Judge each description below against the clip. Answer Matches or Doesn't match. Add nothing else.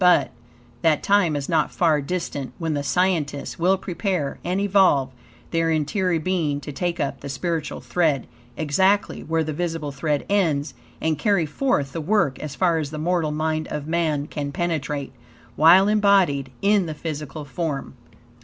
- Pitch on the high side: Doesn't match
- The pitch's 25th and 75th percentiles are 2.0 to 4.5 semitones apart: Matches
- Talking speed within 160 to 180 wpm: Matches